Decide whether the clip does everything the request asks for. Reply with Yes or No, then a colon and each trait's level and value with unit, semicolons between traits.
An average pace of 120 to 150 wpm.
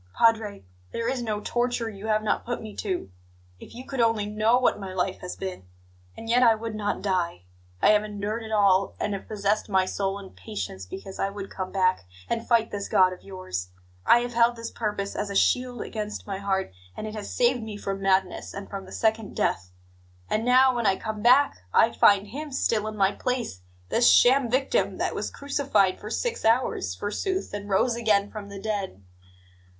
No: fast, 205 wpm